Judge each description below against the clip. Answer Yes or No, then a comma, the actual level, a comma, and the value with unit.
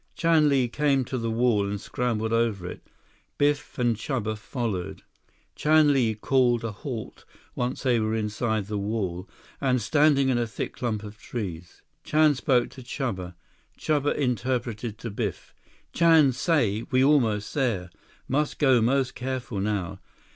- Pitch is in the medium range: No, low, 120 Hz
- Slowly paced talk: No, average, 150 wpm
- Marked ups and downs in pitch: No, average, 4.0 semitones